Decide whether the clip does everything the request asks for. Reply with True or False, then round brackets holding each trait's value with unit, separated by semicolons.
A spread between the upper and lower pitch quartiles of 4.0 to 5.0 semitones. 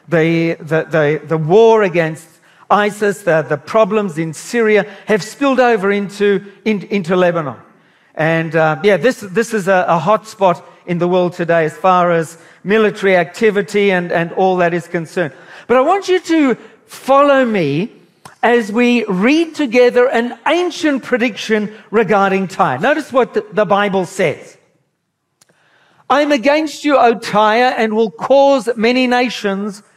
False (5.5 semitones)